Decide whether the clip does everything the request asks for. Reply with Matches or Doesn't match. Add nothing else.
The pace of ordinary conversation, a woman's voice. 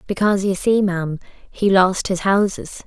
Matches